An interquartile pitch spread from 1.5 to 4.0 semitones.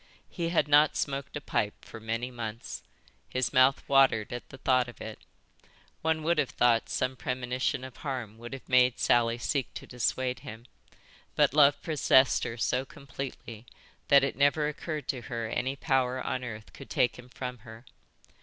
Yes: narrow, 2.6 semitones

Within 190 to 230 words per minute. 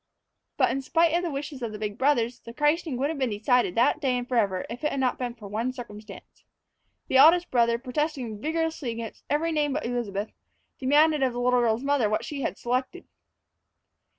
Yes: fast, 205 wpm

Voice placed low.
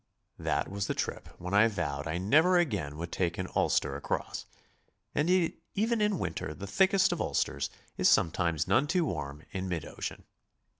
Yes: very low, 95 Hz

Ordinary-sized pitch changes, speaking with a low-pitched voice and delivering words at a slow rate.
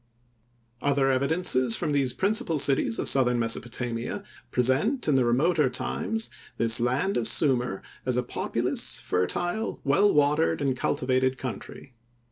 Yes: average, 4.0 semitones; low, 130 Hz; slow, 130 wpm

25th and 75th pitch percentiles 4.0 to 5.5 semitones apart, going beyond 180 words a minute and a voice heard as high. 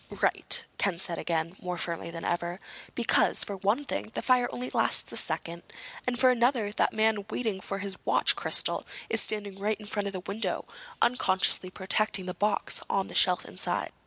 No: average, 3.3 semitones; average, 190 wpm; high, 200 Hz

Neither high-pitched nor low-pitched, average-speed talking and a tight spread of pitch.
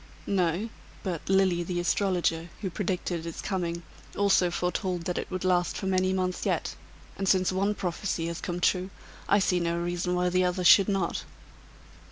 Yes: medium, 180 Hz; average, 175 wpm; narrow, 1.6 semitones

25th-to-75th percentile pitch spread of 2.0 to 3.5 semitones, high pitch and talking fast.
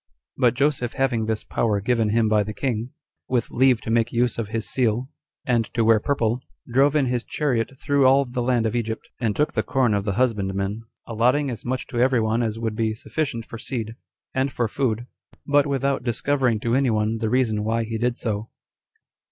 No: average, 2.8 semitones; low, 120 Hz; fast, 210 wpm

